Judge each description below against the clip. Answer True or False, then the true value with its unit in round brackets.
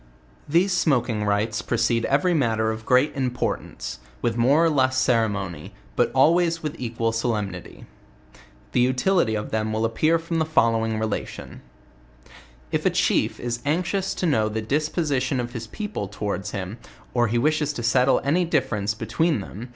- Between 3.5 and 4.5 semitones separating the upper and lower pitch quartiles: False (5.6 semitones)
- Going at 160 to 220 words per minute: True (175 wpm)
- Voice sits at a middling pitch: False (120 Hz)